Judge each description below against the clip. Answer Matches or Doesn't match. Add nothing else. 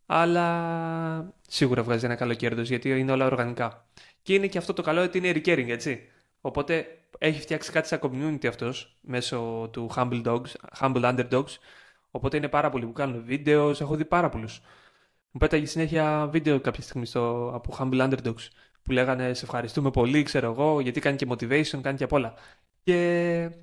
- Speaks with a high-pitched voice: Doesn't match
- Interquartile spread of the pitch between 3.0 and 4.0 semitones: Doesn't match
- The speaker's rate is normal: Doesn't match